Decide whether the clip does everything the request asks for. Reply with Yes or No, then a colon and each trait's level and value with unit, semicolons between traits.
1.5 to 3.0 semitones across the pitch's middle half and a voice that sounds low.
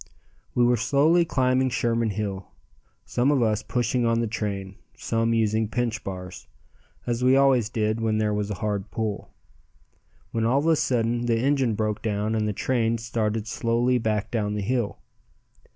Yes: narrow, 2.4 semitones; low, 115 Hz